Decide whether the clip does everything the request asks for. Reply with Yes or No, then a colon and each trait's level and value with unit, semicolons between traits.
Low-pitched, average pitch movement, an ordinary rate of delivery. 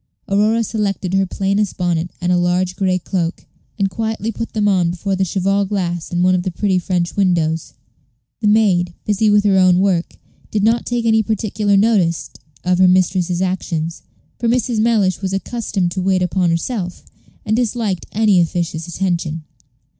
No: high, 190 Hz; average, 3.0 semitones; average, 170 wpm